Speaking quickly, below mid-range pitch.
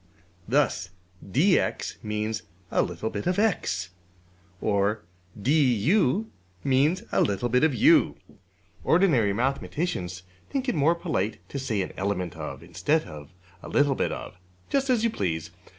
No: slow, 135 wpm; low, 120 Hz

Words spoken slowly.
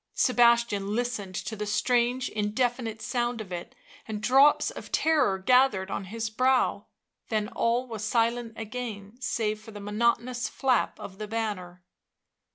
No: average, 145 wpm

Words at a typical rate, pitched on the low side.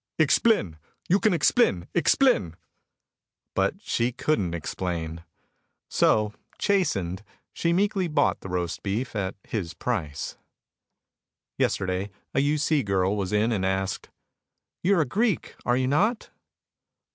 No: slow, 125 wpm; low, 110 Hz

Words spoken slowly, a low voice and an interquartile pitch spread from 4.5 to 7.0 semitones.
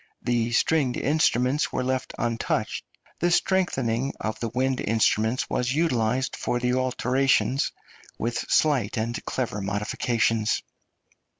No: slow, 115 wpm; low, 125 Hz; average, 2.7 semitones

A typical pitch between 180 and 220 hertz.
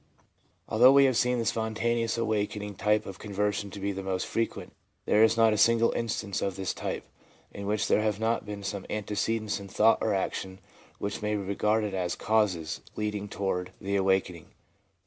No: low, 105 Hz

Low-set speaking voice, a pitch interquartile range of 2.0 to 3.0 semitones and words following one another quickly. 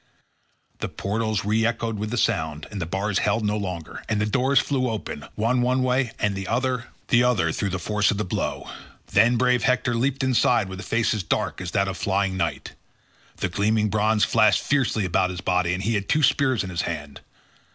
No: low, 105 Hz; average, 4.2 semitones; fast, 210 wpm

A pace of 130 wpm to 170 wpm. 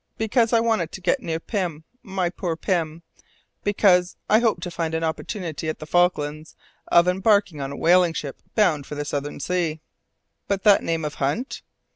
No: average, 180 wpm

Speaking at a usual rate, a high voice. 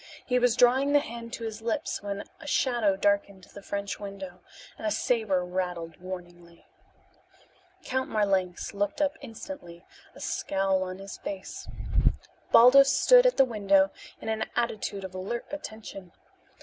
Yes: average, 150 wpm; high, 205 Hz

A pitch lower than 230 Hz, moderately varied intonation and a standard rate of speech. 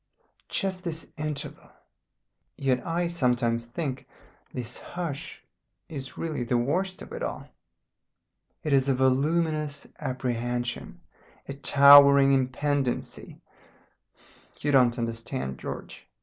No: medium, 140 Hz; average, 3.6 semitones; slow, 105 wpm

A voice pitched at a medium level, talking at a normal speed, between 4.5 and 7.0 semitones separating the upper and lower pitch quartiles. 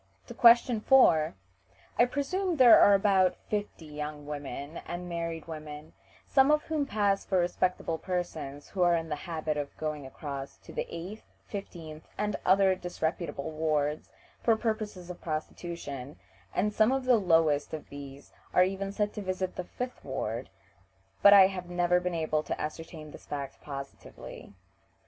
Yes: medium, 175 Hz; average, 160 wpm; average, 4.8 semitones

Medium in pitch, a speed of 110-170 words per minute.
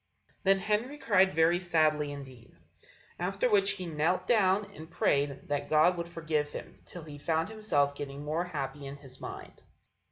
Yes: medium, 160 Hz; average, 165 wpm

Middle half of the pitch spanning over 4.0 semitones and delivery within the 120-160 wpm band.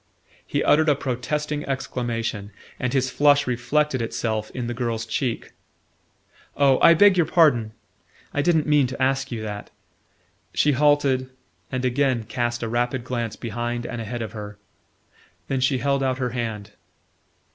No: average, 3.3 semitones; average, 155 wpm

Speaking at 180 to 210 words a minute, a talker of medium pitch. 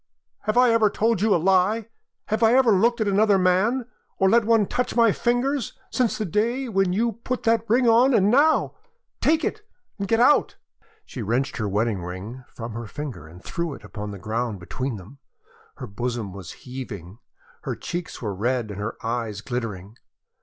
Yes: average, 190 wpm; medium, 180 Hz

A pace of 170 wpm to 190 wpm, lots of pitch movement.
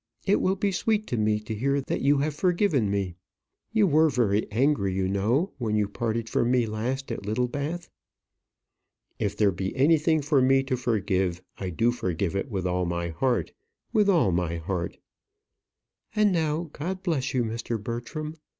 Yes: average, 175 wpm; wide, 7.2 semitones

